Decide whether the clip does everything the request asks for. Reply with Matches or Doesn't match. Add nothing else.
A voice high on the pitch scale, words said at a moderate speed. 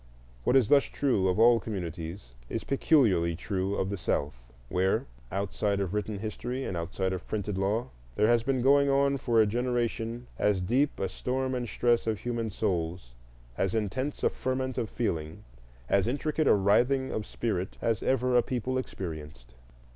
Doesn't match